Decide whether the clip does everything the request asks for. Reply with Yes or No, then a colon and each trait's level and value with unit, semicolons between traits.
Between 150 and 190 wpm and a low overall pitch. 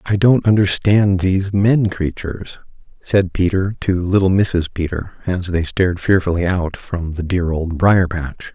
Yes: average, 160 wpm; very low, 90 Hz